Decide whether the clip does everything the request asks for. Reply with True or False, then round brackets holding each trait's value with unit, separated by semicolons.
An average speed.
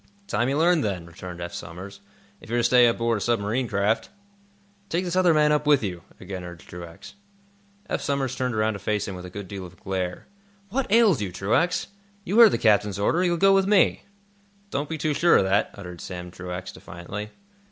False (210 wpm)